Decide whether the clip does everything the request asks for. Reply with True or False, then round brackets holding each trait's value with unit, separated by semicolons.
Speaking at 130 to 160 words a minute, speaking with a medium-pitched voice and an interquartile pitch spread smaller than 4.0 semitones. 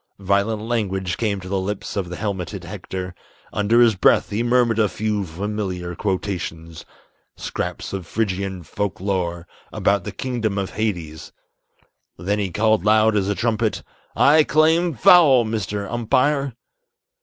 False (145 wpm; 105 Hz; 3.2 semitones)